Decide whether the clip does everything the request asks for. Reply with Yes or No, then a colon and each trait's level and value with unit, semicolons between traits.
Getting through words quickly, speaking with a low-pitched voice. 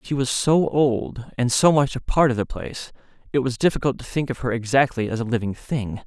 Yes: fast, 240 wpm; low, 130 Hz